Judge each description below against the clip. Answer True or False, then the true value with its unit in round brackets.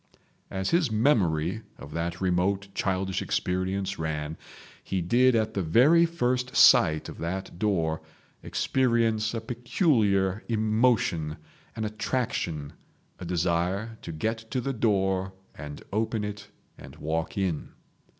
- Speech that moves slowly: True (125 wpm)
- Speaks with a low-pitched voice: True (100 Hz)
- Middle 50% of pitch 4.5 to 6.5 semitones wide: True (4.8 semitones)